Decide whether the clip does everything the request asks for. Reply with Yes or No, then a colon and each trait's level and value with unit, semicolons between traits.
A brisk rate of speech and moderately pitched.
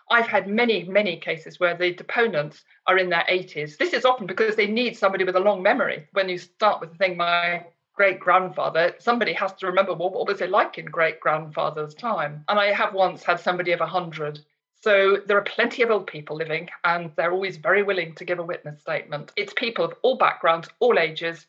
Yes: fast, 215 wpm; medium, 180 Hz